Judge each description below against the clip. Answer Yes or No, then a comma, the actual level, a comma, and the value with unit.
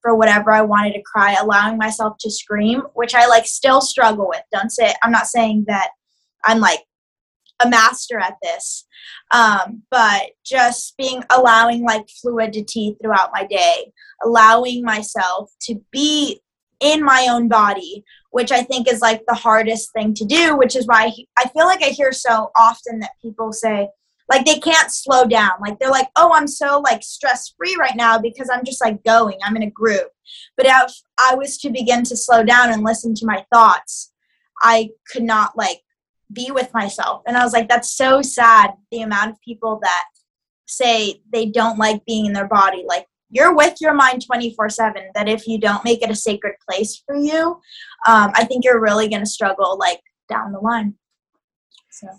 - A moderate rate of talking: Yes, average, 190 wpm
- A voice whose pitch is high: Yes, high, 230 Hz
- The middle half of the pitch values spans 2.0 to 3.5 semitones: Yes, average, 3.0 semitones